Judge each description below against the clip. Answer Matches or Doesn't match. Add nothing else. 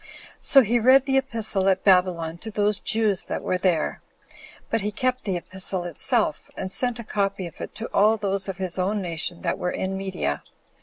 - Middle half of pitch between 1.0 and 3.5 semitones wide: Matches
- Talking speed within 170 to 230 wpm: Matches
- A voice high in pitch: Matches